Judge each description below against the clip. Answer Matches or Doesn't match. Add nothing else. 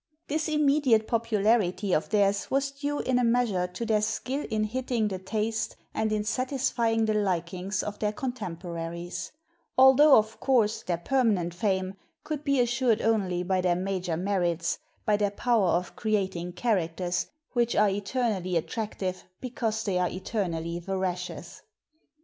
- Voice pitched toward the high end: Matches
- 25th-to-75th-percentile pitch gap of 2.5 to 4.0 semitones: Doesn't match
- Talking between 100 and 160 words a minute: Matches